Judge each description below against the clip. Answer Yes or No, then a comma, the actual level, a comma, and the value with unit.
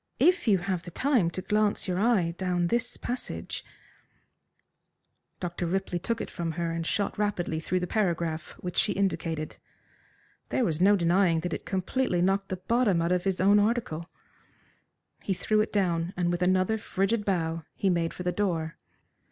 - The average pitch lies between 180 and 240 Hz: Yes, medium, 185 Hz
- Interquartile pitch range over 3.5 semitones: No, average, 3.2 semitones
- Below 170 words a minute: No, average, 175 wpm